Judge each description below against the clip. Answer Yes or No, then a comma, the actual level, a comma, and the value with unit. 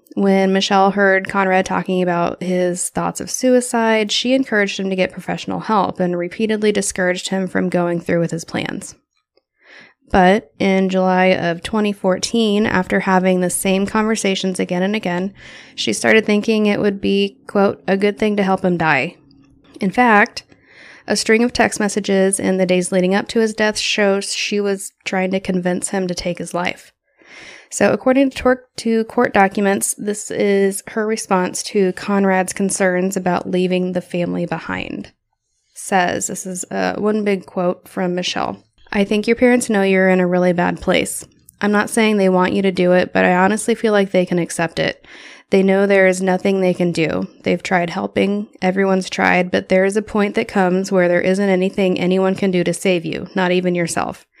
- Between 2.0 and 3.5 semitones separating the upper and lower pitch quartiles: Yes, narrow, 2.4 semitones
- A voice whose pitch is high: Yes, high, 195 Hz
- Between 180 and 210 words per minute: Yes, average, 185 wpm